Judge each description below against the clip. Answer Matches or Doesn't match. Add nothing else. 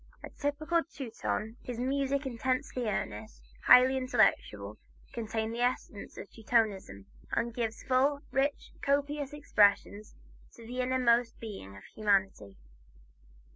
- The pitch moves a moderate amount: Matches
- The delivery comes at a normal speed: Doesn't match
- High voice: Matches